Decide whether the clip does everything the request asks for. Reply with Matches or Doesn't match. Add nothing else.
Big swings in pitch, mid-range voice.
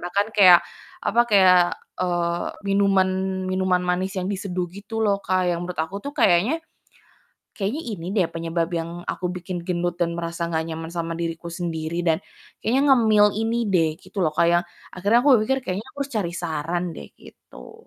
Doesn't match